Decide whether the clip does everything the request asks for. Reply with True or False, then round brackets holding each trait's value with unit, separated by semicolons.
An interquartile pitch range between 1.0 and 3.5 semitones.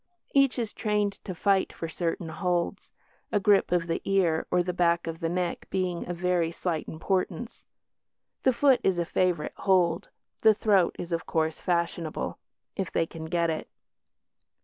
True (2.6 semitones)